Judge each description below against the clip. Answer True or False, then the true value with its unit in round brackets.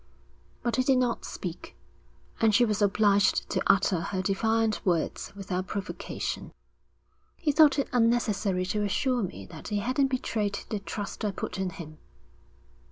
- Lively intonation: False (3.8 semitones)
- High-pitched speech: True (210 Hz)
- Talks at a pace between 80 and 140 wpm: False (155 wpm)